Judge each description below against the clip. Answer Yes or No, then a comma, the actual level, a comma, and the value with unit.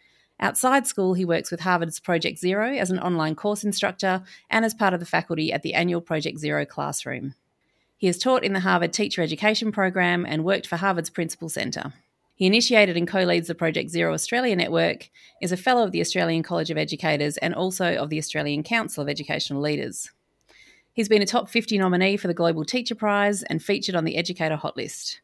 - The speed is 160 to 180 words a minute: No, average, 200 wpm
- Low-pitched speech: No, medium, 180 Hz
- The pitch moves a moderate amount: Yes, average, 4.0 semitones